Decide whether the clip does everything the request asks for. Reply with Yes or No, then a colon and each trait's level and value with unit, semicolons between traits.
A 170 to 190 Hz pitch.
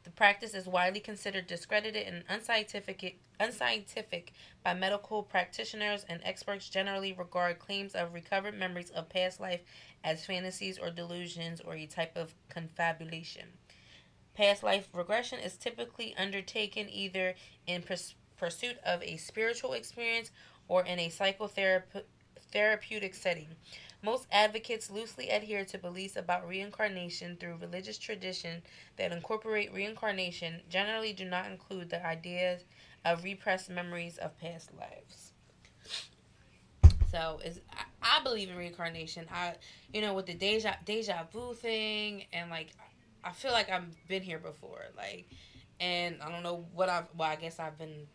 Yes: medium, 185 Hz